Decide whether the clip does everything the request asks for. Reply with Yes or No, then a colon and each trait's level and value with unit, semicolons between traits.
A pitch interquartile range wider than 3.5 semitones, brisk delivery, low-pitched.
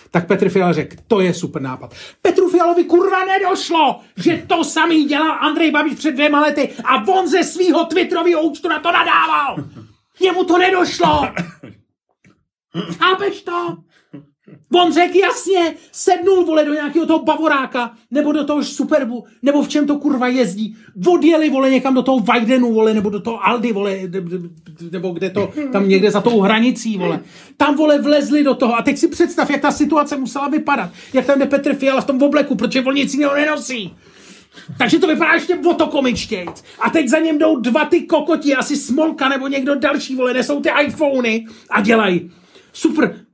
No: average, 5.2 semitones; fast, 180 wpm; very high, 285 Hz